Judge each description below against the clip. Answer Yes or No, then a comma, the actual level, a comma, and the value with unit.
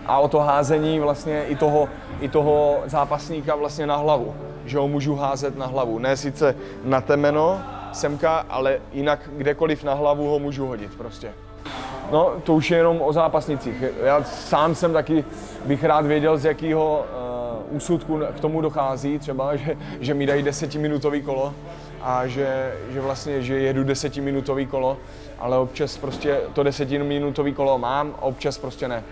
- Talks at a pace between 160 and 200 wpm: Yes, average, 165 wpm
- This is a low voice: No, medium, 145 Hz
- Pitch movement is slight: Yes, narrow, 1.9 semitones